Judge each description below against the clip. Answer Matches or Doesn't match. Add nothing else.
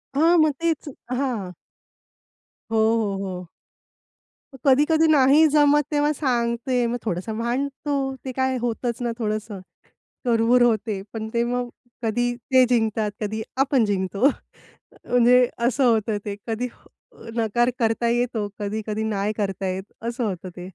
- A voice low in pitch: Doesn't match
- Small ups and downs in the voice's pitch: Doesn't match